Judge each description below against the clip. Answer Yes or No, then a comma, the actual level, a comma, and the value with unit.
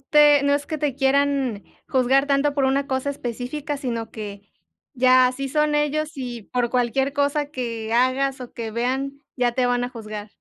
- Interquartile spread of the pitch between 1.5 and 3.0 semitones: Yes, average, 2.7 semitones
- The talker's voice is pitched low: No, very high, 265 Hz